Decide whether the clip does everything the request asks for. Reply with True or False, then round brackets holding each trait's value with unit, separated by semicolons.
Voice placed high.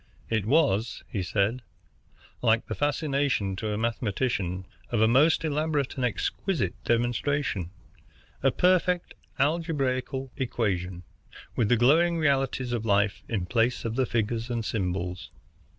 False (120 Hz)